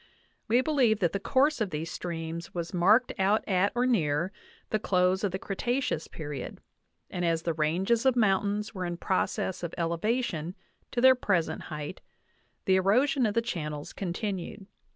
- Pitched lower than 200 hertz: Yes, high, 190 Hz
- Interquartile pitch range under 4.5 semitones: No, average, 5.1 semitones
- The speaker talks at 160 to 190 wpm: Yes, average, 170 wpm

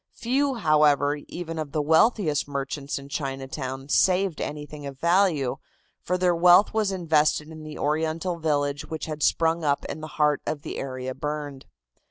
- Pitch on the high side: No, medium, 150 Hz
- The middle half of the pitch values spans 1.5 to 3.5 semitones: Yes, average, 2.9 semitones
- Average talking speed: Yes, average, 165 wpm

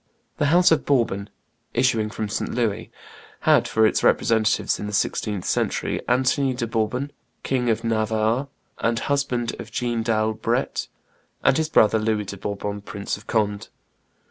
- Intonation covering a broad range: No, narrow, 2.6 semitones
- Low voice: Yes, low, 110 Hz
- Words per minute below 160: Yes, average, 150 wpm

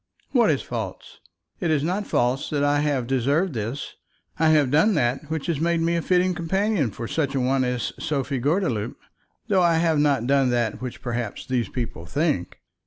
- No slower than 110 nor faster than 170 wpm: No, average, 190 wpm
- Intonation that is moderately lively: Yes, average, 4.8 semitones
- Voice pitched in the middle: Yes, medium, 145 Hz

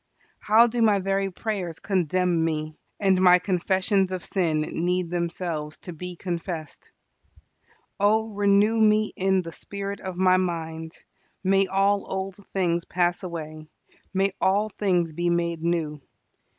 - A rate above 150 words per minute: No, average, 140 wpm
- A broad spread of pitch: No, narrow, 2.5 semitones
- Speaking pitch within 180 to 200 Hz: Yes, medium, 185 Hz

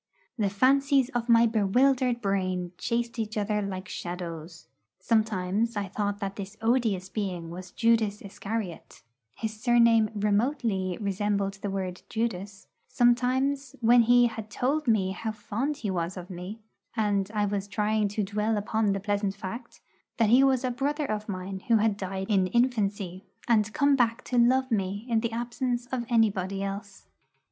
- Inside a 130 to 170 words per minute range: Yes, average, 160 wpm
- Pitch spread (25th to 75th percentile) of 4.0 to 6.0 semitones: No, average, 3.3 semitones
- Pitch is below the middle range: No, high, 215 Hz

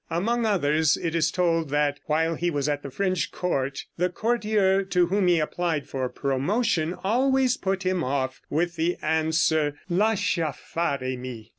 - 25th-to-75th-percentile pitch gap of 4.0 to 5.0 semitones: Yes, average, 4.5 semitones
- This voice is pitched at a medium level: Yes, medium, 165 Hz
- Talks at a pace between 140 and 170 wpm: Yes, average, 160 wpm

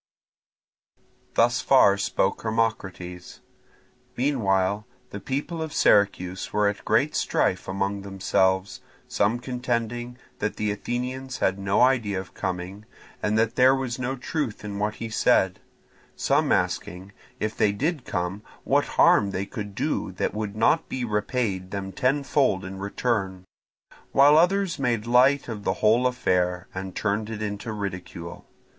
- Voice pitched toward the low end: Yes, low, 105 Hz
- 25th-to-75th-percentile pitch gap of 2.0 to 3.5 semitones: No, average, 4.3 semitones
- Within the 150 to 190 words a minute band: No, average, 140 wpm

